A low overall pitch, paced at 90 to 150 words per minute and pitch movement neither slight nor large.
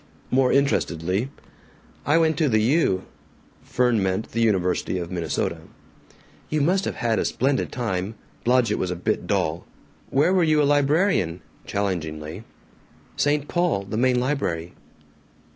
No: low, 115 Hz; average, 140 wpm; wide, 7.8 semitones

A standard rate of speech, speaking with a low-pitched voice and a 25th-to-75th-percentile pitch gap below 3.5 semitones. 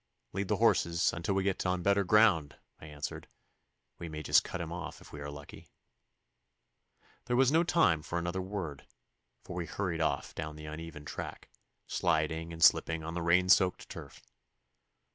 Yes: average, 175 wpm; very low, 85 Hz; average, 3.1 semitones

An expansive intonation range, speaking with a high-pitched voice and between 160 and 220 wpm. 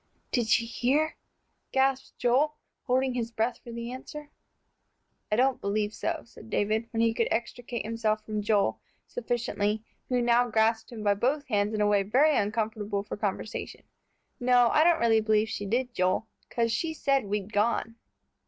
No: average, 2.7 semitones; high, 230 Hz; average, 170 wpm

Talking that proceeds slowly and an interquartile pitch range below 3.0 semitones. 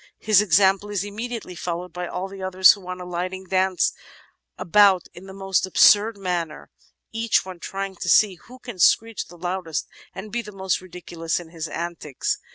No: average, 175 wpm; narrow, 2.4 semitones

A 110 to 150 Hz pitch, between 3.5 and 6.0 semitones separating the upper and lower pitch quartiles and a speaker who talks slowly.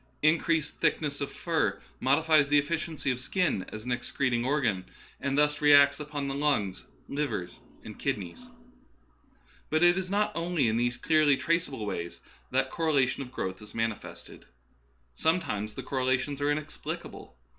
No: medium, 140 Hz; average, 4.4 semitones; average, 155 wpm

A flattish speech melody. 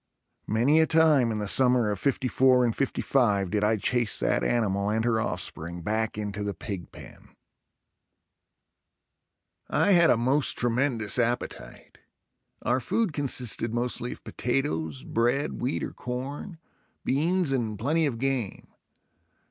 No: average, 4.1 semitones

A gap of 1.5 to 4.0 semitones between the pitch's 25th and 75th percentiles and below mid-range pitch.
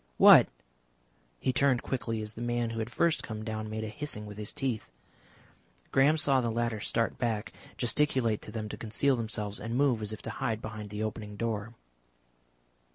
Yes: narrow, 2.5 semitones; low, 115 Hz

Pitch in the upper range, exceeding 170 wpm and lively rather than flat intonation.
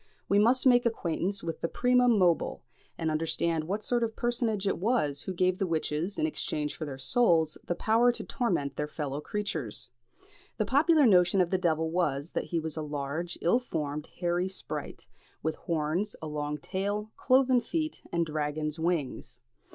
No: medium, 175 Hz; average, 180 wpm; wide, 5.9 semitones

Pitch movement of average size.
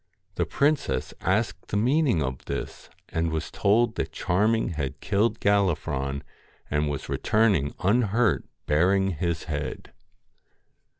No: wide, 5.9 semitones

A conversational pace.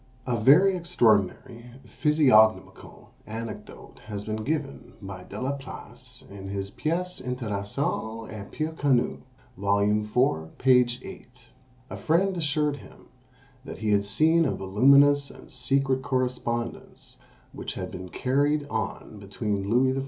No: slow, 130 wpm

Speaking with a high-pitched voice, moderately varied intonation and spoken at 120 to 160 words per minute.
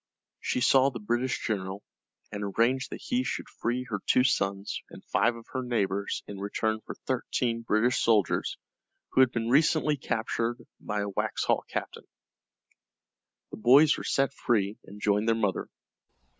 No: low, 115 Hz; average, 3.7 semitones; average, 155 wpm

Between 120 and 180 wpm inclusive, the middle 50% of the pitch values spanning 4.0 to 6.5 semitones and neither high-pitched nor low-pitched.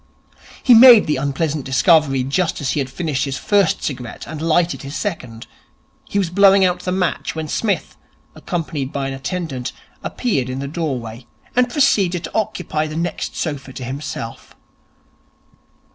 Yes: average, 160 wpm; average, 5.2 semitones; medium, 155 Hz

